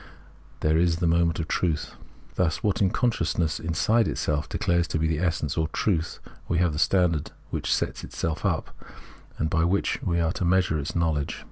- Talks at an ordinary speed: Yes, average, 190 wpm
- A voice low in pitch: Yes, very low, 85 Hz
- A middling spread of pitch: No, narrow, 1.9 semitones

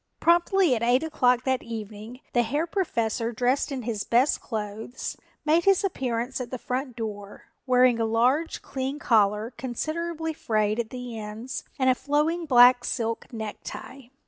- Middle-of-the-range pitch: No, very high, 250 Hz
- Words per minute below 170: Yes, average, 155 wpm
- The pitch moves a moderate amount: Yes, average, 3.8 semitones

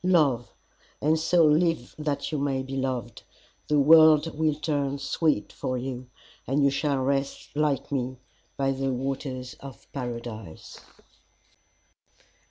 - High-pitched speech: No, medium, 140 Hz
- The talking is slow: Yes, slow, 130 wpm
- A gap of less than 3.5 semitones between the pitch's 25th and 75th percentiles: Yes, average, 2.7 semitones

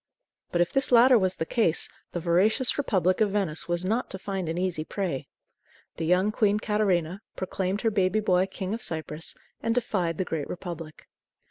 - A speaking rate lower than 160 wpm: No, average, 185 wpm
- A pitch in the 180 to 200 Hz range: Yes, medium, 185 Hz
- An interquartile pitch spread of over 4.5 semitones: No, average, 3.5 semitones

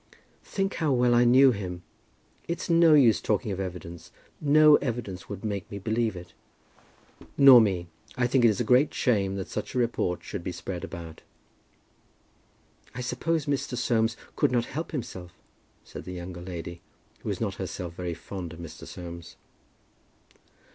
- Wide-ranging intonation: Yes, wide, 6.0 semitones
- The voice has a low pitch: Yes, low, 110 Hz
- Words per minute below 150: No, average, 165 wpm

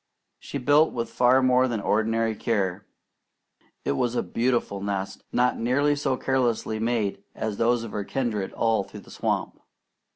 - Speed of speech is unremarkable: Yes, average, 160 wpm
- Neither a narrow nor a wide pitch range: Yes, average, 3.2 semitones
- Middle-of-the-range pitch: No, low, 115 Hz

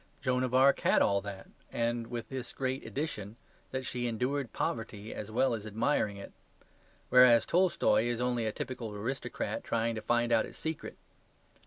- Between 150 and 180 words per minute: Yes, average, 170 wpm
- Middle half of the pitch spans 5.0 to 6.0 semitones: No, average, 2.7 semitones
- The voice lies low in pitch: Yes, low, 120 Hz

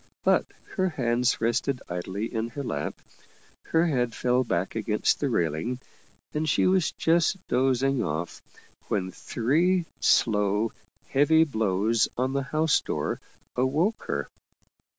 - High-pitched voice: No, low, 125 Hz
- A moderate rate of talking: No, slow, 130 wpm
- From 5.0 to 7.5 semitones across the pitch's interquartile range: Yes, wide, 5.4 semitones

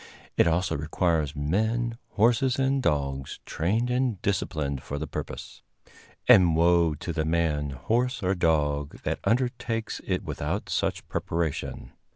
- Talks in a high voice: No, very low, 85 Hz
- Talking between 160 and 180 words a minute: No, slow, 135 wpm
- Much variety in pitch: Yes, wide, 7.2 semitones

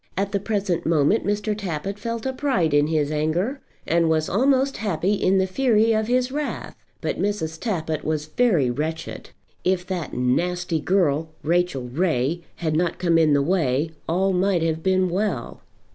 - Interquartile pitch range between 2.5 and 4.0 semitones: No, average, 4.5 semitones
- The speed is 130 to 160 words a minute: No, average, 170 wpm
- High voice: No, medium, 180 Hz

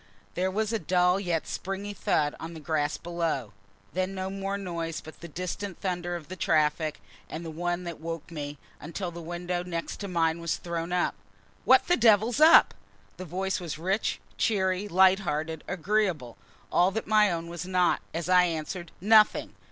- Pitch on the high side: No, medium, 175 Hz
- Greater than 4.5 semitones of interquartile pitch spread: No, average, 2.7 semitones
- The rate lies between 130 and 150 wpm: No, average, 175 wpm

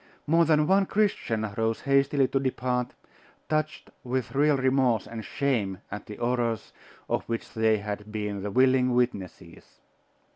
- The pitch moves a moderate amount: Yes, average, 4.0 semitones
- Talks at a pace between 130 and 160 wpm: Yes, average, 145 wpm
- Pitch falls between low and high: No, low, 125 Hz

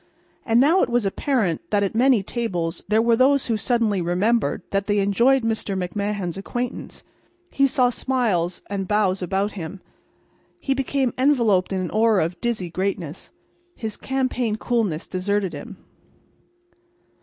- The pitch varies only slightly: No, average, 4.2 semitones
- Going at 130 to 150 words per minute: Yes, average, 145 wpm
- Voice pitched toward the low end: No, high, 210 Hz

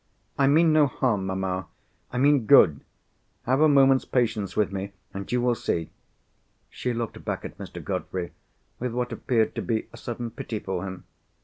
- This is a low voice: Yes, low, 115 Hz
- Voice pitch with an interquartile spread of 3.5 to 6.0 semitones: Yes, average, 5.0 semitones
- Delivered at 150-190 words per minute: Yes, average, 175 wpm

